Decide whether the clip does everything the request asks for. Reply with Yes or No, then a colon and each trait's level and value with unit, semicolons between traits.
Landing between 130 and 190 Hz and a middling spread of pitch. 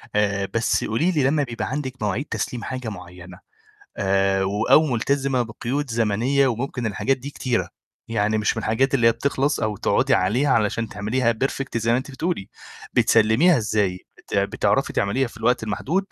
No: low, 115 Hz; average, 4.3 semitones